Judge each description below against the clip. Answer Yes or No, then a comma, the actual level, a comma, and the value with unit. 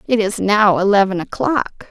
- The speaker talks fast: No, average, 155 wpm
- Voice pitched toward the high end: Yes, high, 205 Hz